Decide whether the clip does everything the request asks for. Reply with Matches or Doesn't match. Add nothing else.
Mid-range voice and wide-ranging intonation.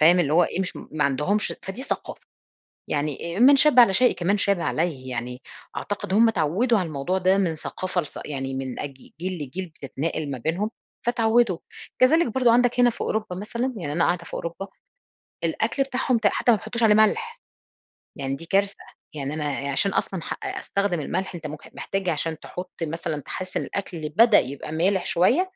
Matches